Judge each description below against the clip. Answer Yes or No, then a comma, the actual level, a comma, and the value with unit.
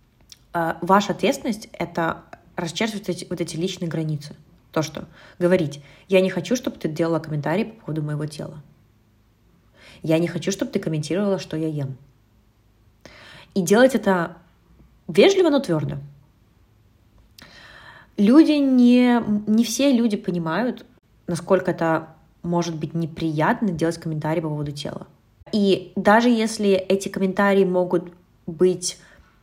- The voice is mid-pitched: Yes, medium, 175 Hz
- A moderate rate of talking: Yes, average, 120 wpm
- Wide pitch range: No, average, 4.6 semitones